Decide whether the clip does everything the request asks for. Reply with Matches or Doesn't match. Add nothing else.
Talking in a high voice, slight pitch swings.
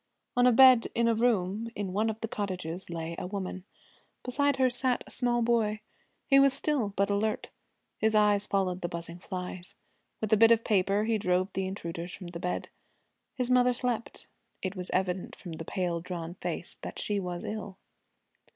Doesn't match